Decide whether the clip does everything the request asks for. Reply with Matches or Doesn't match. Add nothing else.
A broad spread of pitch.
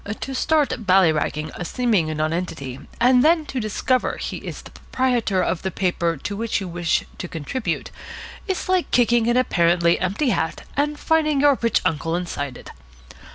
Matches